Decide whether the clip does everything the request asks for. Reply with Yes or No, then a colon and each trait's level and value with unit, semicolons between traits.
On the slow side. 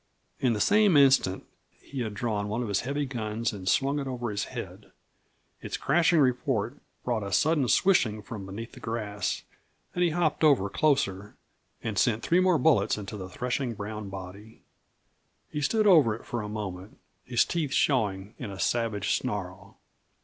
No: average, 170 wpm